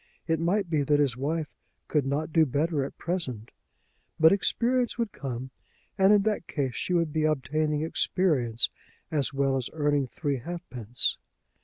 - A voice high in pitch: No, medium, 150 Hz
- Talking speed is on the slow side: No, average, 160 wpm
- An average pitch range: Yes, average, 4.0 semitones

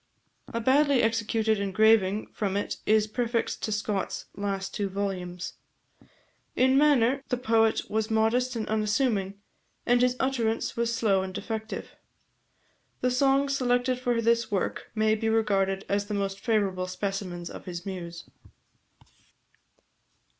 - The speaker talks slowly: Yes, slow, 130 wpm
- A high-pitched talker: Yes, high, 220 Hz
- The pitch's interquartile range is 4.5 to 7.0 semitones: No, average, 3.5 semitones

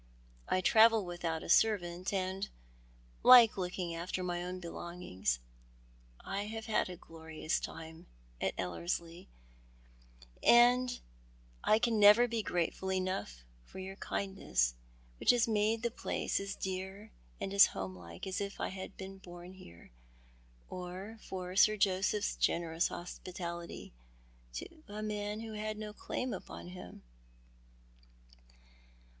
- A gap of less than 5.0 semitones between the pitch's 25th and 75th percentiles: Yes, average, 3.4 semitones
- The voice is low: No, high, 190 Hz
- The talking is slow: Yes, slow, 130 wpm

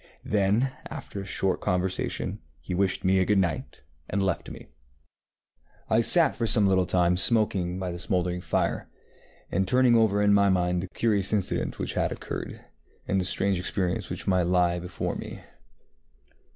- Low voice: Yes, very low, 95 Hz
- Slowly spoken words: No, average, 165 wpm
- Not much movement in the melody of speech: Yes, narrow, 2.3 semitones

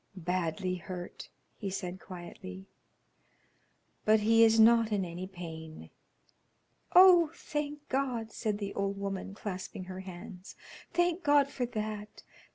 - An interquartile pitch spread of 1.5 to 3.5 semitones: No, average, 4.0 semitones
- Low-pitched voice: No, high, 200 Hz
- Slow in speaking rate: Yes, slow, 125 wpm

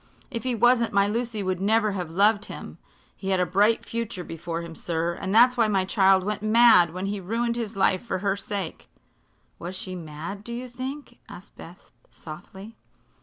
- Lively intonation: No, average, 3.9 semitones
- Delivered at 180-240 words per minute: Yes, average, 190 wpm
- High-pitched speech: Yes, high, 200 Hz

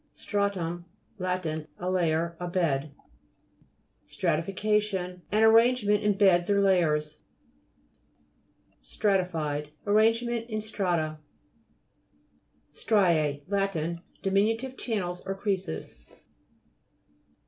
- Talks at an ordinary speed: No, slow, 80 wpm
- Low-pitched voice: No, high, 190 Hz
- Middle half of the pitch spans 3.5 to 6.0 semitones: Yes, average, 3.9 semitones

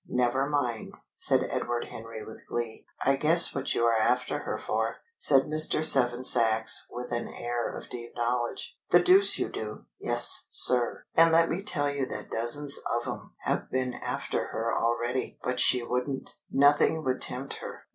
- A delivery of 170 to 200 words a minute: Yes, average, 175 wpm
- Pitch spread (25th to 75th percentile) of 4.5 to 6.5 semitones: No, average, 3.3 semitones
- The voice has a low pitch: Yes, low, 125 Hz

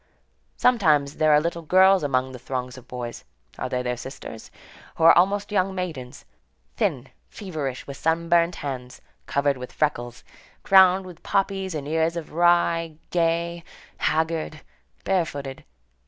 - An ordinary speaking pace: No, slow, 130 wpm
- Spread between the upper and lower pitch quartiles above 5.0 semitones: No, average, 4.7 semitones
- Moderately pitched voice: Yes, medium, 160 Hz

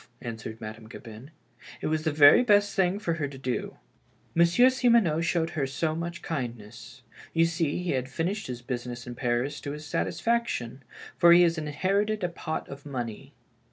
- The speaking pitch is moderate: Yes, medium, 150 Hz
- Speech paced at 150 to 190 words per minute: Yes, average, 185 wpm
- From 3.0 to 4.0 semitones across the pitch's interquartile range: No, wide, 5.6 semitones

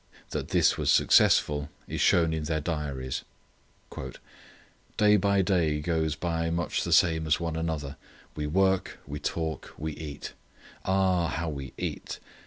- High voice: No, very low, 80 Hz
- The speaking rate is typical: Yes, average, 145 wpm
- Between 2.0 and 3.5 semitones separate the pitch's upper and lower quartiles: Yes, narrow, 2.5 semitones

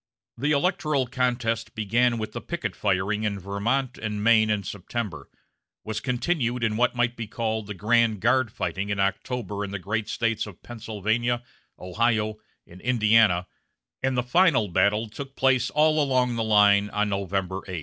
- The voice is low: Yes, low, 110 Hz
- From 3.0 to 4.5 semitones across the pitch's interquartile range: Yes, average, 3.3 semitones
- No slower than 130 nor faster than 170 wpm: Yes, average, 165 wpm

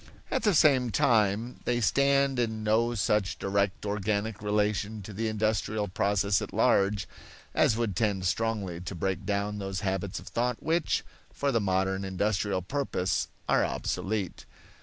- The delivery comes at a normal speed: Yes, average, 150 wpm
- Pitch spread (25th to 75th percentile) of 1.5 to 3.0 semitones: Yes, average, 2.7 semitones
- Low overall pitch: Yes, low, 105 Hz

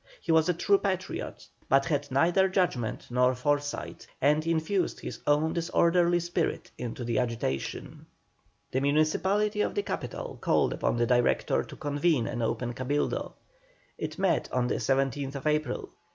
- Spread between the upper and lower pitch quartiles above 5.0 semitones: Yes, wide, 5.4 semitones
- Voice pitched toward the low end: No, medium, 145 Hz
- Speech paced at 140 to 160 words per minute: Yes, average, 150 wpm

